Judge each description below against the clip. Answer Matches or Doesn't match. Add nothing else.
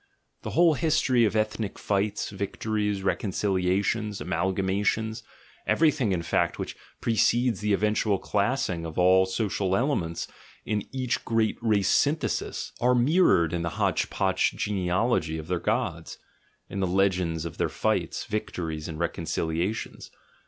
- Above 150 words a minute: Doesn't match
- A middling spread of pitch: Matches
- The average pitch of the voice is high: Doesn't match